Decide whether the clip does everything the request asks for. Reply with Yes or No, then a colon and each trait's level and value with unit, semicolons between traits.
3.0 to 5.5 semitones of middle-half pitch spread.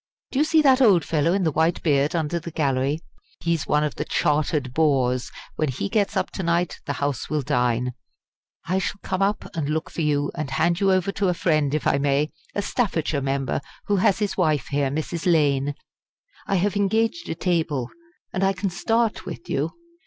Yes: average, 5.0 semitones